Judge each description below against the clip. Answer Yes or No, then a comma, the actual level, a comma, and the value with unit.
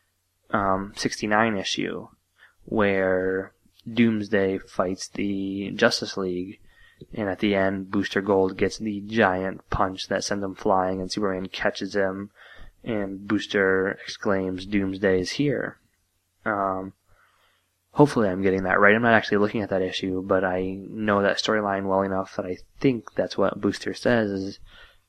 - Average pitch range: No, narrow, 1.7 semitones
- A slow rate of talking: No, average, 145 wpm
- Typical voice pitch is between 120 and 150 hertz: No, very low, 95 Hz